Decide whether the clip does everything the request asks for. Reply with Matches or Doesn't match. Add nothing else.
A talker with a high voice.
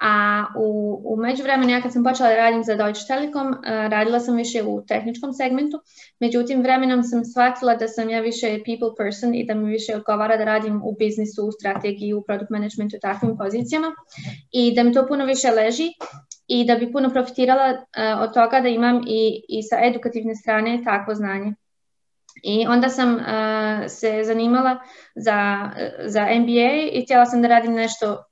Matches